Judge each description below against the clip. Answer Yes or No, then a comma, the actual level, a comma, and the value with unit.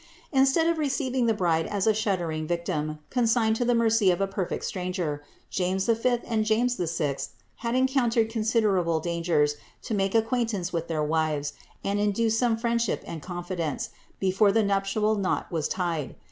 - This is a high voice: Yes, high, 200 Hz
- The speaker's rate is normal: Yes, average, 165 wpm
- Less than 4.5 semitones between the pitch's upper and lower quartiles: No, average, 5.1 semitones